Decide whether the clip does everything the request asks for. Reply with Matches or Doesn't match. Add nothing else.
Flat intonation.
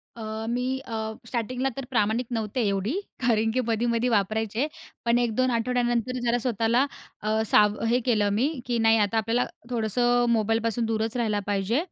Matches